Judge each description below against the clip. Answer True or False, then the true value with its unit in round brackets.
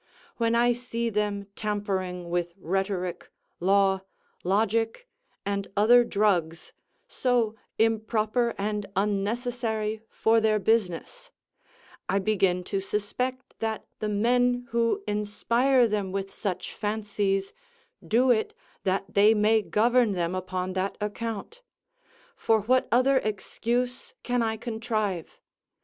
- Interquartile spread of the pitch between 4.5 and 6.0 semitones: False (3.1 semitones)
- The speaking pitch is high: True (215 Hz)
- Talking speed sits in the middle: False (115 wpm)